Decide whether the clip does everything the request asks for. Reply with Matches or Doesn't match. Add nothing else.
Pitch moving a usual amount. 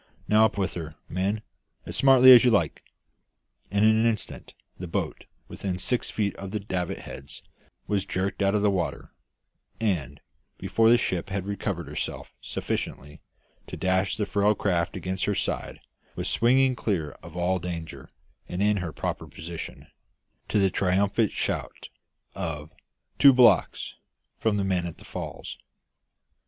Matches